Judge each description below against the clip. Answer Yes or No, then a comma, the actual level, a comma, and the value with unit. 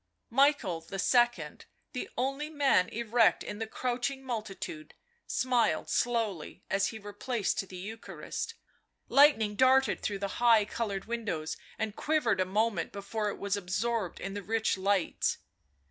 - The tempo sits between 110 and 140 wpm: Yes, slow, 135 wpm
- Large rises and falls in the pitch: No, average, 3.6 semitones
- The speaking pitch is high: Yes, high, 220 Hz